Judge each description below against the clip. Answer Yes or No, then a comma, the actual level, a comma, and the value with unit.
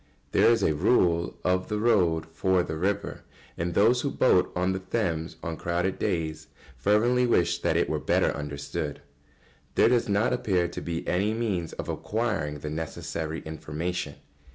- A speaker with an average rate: Yes, average, 170 wpm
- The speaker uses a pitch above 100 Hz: No, very low, 90 Hz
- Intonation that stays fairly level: No, average, 4.6 semitones